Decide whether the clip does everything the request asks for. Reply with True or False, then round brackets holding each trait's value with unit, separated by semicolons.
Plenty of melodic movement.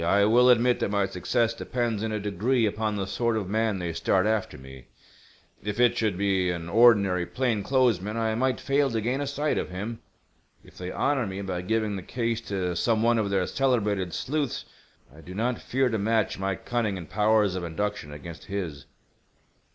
False (3.7 semitones)